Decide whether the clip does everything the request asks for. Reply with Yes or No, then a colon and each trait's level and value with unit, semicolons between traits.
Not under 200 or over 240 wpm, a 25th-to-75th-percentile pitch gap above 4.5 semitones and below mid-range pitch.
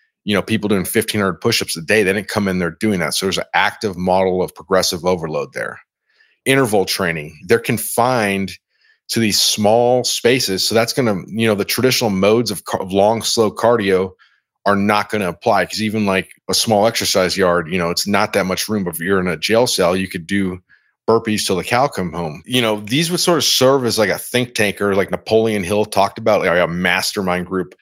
No: fast, 205 wpm; average, 3.5 semitones; low, 105 Hz